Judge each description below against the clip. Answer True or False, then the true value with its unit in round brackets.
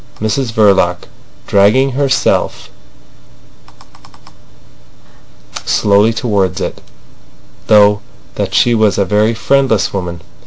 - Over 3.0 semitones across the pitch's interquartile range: False (2.6 semitones)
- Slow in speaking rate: True (85 wpm)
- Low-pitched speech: True (105 Hz)